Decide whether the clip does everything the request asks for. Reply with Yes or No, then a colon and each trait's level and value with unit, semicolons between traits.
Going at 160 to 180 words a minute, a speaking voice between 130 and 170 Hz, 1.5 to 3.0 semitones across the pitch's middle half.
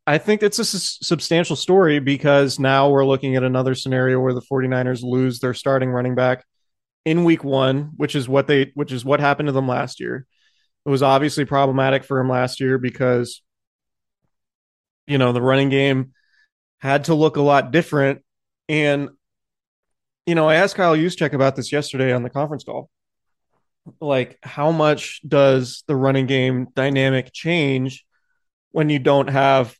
Yes: average, 170 wpm; low, 135 Hz; narrow, 2.6 semitones